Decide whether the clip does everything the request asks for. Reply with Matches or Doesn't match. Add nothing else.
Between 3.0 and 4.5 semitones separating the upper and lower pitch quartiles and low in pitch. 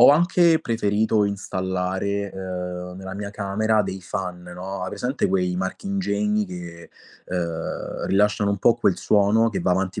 Doesn't match